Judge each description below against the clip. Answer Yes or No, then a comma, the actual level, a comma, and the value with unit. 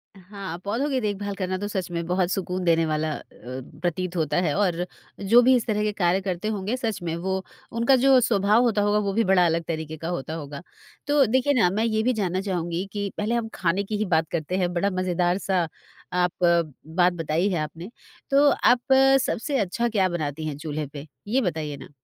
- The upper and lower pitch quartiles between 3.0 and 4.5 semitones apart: Yes, average, 4.1 semitones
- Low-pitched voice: No, medium, 185 Hz